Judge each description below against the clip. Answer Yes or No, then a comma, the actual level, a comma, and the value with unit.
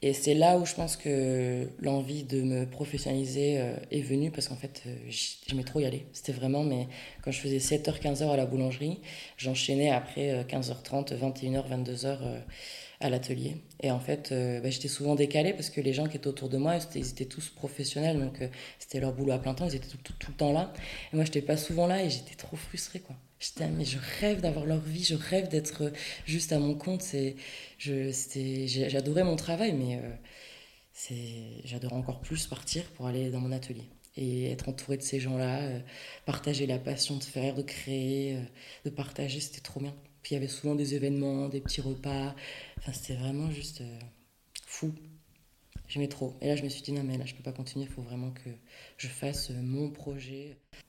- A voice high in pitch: No, medium, 140 Hz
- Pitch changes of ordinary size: No, narrow, 2.1 semitones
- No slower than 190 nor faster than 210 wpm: Yes, average, 205 wpm